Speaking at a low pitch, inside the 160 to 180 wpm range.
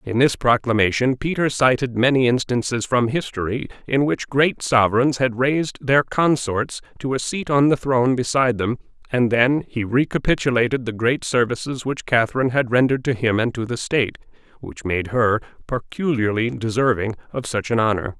Yes: low, 125 Hz; average, 170 wpm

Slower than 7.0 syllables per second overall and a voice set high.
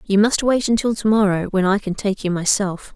Yes: 5.3 syllables/s; high, 205 Hz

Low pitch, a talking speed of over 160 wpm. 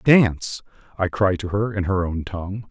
Yes: very low, 95 Hz; average, 200 wpm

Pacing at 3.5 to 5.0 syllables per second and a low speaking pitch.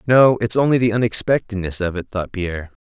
No: 5.8 syllables/s; low, 105 Hz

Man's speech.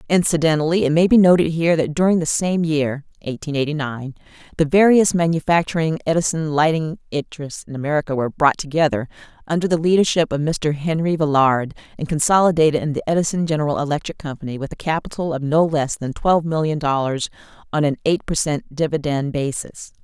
No: female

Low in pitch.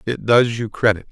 Yes: low, 115 Hz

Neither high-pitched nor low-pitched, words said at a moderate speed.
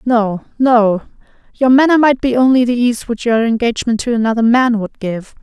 No: high, 235 Hz; average, 190 wpm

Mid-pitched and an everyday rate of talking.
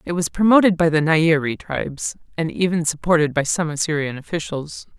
Yes: medium, 160 Hz; average, 170 wpm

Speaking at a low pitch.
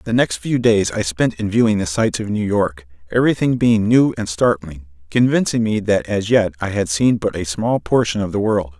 Yes: low, 100 Hz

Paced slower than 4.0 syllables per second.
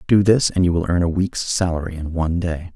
No: 5.8 syllables/s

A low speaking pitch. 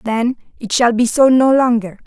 No: high, 240 Hz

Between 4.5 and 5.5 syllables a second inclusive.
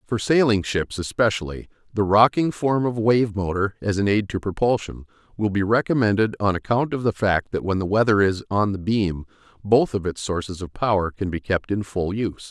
Yes: 5.3 syllables/s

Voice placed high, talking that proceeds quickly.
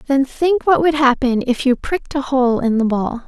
Yes: very high, 265 Hz; fast, 240 wpm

